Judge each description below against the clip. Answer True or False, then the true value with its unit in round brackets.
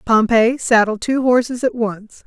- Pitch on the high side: True (235 Hz)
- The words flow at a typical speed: True (160 wpm)